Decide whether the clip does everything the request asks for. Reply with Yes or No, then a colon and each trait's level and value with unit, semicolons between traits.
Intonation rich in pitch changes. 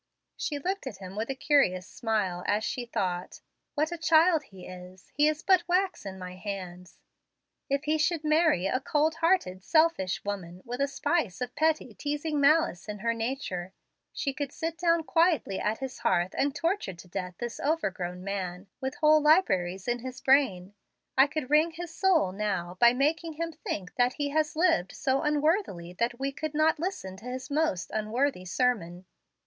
Yes: wide, 8.5 semitones